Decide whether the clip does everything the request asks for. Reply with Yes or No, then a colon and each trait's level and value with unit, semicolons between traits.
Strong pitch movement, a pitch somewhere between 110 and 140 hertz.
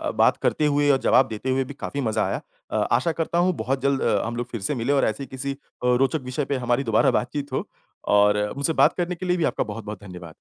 No: average, 4.2 semitones; low, 135 Hz